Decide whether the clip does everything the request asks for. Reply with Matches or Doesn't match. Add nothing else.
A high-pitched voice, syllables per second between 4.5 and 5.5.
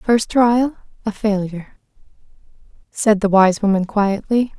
Doesn't match